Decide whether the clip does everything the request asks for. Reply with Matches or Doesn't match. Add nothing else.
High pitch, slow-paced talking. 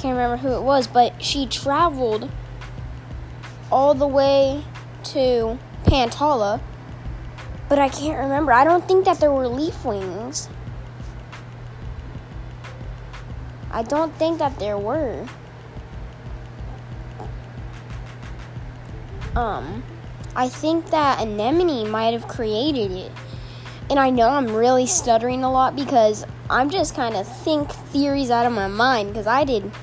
Matches